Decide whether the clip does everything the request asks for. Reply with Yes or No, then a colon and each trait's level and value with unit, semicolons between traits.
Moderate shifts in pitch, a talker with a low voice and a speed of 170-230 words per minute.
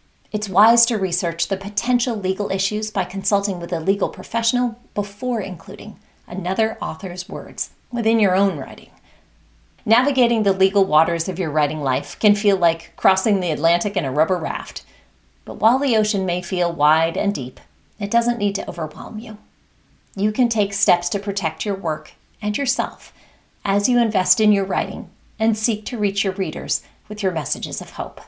No: average, 3.5 semitones; high, 200 Hz; average, 175 wpm